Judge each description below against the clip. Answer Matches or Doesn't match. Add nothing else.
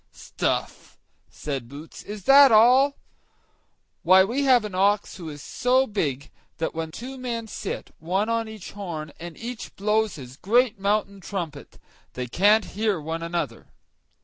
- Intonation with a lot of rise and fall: Matches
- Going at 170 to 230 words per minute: Doesn't match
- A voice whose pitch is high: Matches